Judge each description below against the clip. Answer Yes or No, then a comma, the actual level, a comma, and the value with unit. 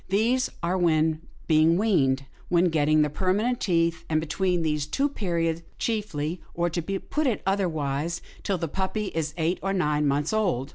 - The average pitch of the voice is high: No, medium, 170 Hz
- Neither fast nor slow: Yes, average, 170 wpm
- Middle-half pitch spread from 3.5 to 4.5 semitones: Yes, average, 3.9 semitones